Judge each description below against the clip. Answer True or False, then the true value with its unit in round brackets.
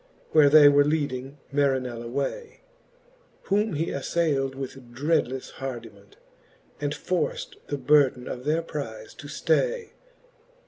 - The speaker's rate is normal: False (120 wpm)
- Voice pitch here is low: False (145 Hz)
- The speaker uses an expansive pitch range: False (3.7 semitones)